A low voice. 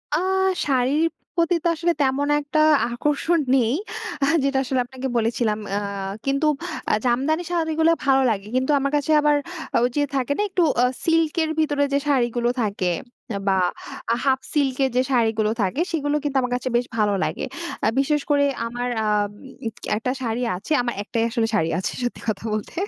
No: very high, 265 Hz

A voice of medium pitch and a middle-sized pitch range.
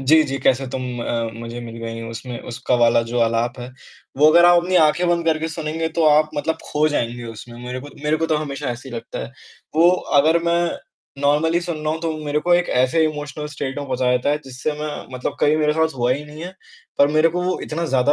Yes: medium, 150 Hz; average, 4.2 semitones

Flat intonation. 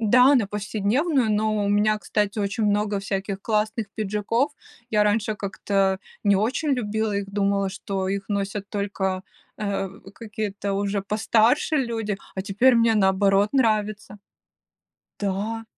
Yes: narrow, 1.8 semitones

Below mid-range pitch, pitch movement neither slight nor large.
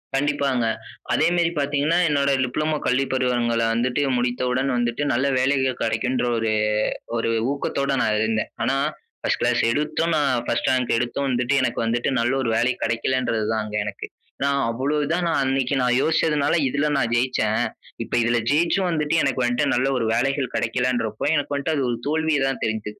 Yes: low, 130 Hz; average, 3.2 semitones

